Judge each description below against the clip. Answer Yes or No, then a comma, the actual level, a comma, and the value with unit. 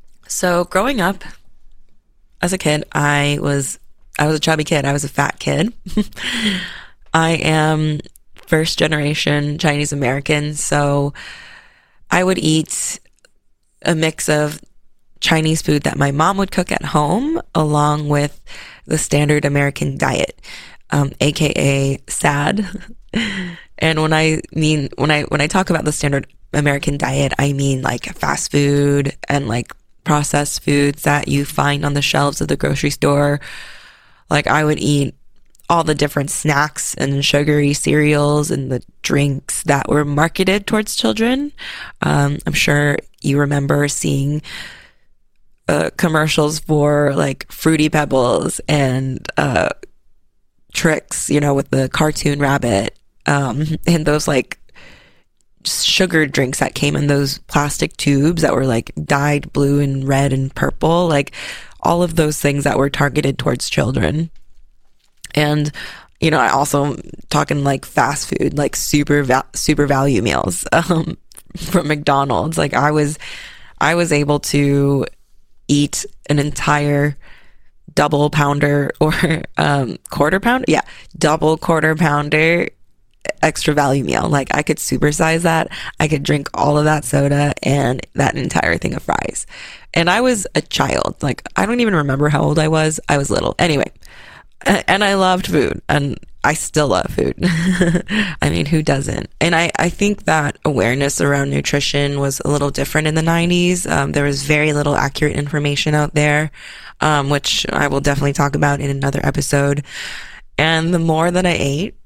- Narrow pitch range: Yes, narrow, 2.1 semitones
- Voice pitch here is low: No, medium, 150 Hz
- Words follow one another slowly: No, average, 150 wpm